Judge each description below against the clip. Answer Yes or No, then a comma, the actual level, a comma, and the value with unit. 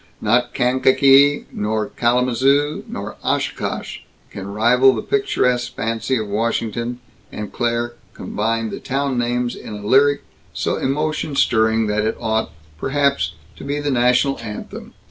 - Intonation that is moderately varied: Yes, average, 3.5 semitones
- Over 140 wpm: No, slow, 135 wpm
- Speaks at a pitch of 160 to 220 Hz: No, low, 120 Hz